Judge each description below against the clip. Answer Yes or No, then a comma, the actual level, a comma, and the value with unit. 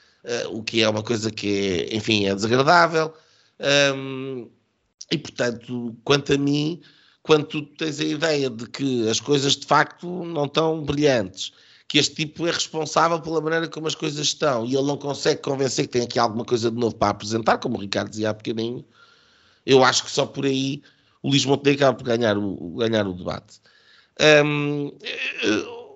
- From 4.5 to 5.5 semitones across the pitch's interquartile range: Yes, average, 4.8 semitones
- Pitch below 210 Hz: Yes, low, 135 Hz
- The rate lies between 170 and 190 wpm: Yes, average, 180 wpm